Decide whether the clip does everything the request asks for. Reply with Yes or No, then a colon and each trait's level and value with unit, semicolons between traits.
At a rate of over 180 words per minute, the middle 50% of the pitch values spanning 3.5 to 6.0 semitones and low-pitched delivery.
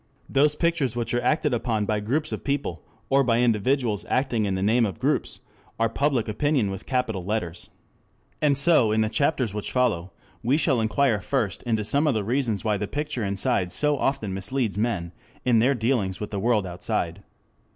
Yes: average, 190 wpm; average, 4.8 semitones; low, 115 Hz